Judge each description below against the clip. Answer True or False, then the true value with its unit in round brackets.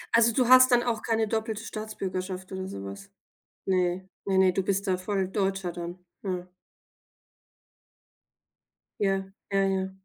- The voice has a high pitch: True (195 Hz)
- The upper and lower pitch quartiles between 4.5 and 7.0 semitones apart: False (2.7 semitones)